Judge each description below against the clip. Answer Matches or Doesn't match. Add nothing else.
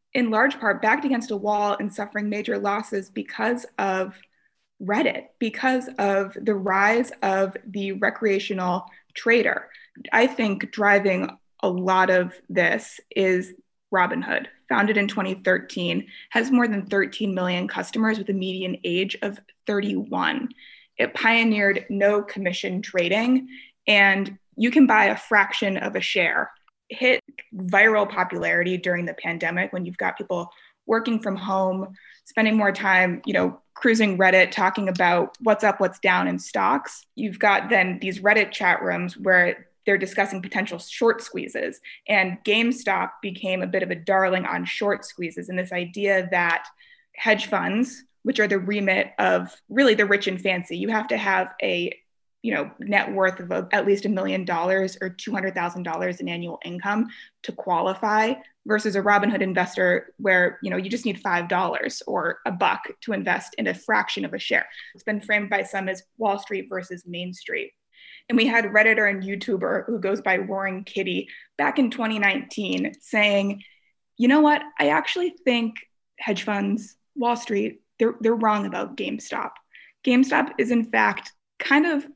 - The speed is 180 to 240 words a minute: Doesn't match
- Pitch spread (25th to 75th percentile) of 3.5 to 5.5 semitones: Doesn't match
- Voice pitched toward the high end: Matches